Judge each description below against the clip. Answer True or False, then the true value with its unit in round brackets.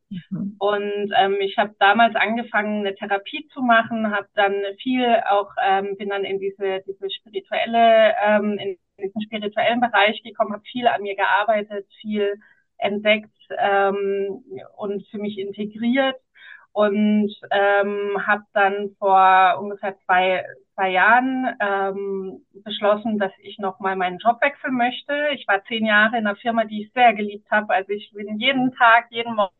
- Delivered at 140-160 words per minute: True (155 wpm)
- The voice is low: False (205 Hz)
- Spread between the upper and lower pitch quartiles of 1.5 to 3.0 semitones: True (2.7 semitones)